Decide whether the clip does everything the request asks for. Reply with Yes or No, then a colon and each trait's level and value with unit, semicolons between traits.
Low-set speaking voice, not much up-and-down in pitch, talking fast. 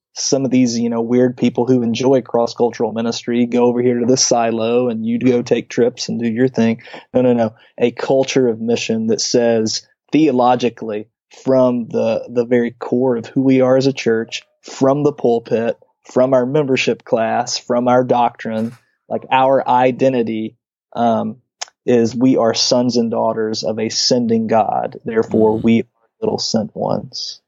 No: low, 120 Hz; narrow, 2.0 semitones; average, 170 wpm